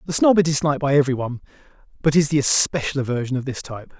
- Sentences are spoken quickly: Yes, fast, 225 wpm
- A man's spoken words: Yes, male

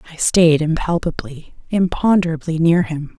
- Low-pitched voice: No, medium, 165 Hz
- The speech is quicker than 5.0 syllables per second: No, 4.7 syllables/s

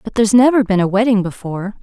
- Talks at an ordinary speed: No, fast, 230 wpm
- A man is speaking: No, female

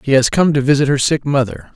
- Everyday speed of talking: No, fast, 275 wpm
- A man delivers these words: Yes, male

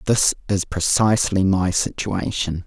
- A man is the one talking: Yes, male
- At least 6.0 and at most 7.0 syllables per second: No, 4.2 syllables/s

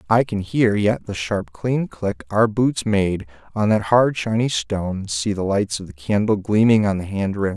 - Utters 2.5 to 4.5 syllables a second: Yes, 4.4 syllables/s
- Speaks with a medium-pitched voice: No, low, 105 Hz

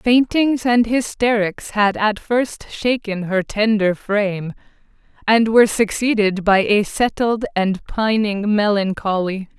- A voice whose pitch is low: No, high, 215 Hz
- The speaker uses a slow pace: Yes, slow, 120 wpm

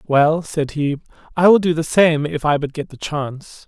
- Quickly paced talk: Yes, fast, 230 wpm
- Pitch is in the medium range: Yes, medium, 155 Hz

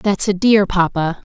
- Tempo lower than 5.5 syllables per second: Yes, 4.1 syllables/s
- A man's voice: No, female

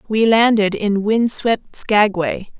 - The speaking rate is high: No, average, 140 wpm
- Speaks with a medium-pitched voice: No, high, 210 Hz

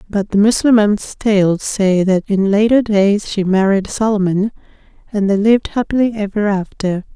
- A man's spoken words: No, female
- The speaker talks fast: No, average, 150 wpm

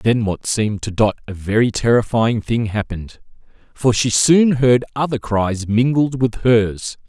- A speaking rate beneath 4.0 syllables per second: No, 4.4 syllables/s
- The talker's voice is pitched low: Yes, low, 115 Hz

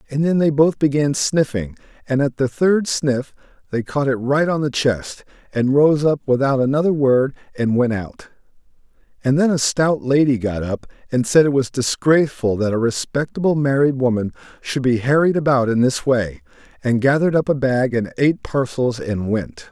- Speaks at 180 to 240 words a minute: Yes, average, 185 wpm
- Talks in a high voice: No, low, 135 Hz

